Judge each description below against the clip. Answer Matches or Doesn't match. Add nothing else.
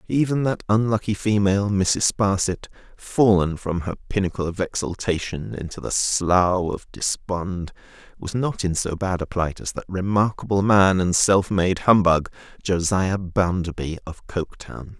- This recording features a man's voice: Matches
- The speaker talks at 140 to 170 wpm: Matches